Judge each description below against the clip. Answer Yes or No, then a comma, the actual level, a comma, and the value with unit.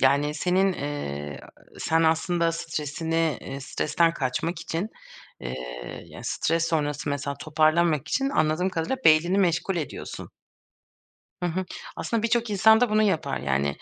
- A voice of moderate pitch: Yes, medium, 165 Hz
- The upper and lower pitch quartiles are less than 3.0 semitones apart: No, average, 3.5 semitones